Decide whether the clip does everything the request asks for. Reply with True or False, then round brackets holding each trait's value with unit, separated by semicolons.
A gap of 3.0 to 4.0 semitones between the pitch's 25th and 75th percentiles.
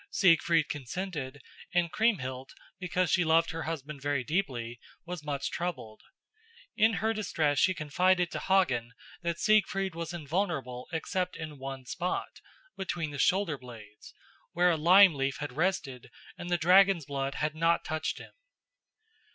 False (4.6 semitones)